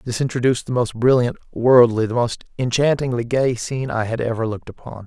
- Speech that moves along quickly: No, average, 190 wpm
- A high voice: No, low, 120 Hz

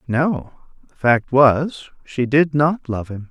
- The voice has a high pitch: No, low, 135 Hz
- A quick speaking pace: No, average, 165 wpm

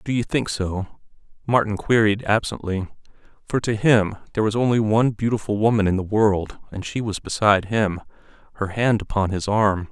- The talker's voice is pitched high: No, low, 105 Hz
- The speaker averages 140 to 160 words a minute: No, average, 175 wpm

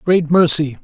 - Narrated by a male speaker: Yes, male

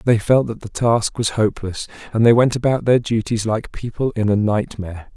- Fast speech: Yes, fast, 210 wpm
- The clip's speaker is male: Yes, male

